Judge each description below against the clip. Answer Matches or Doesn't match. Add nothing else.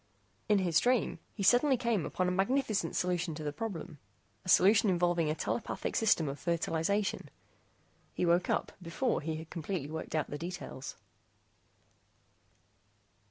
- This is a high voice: Doesn't match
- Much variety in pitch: Doesn't match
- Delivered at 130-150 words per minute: Matches